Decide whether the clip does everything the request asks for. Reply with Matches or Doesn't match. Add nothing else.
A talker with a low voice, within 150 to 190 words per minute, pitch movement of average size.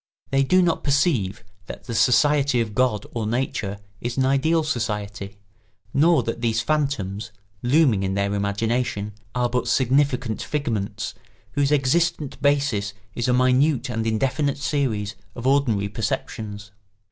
Doesn't match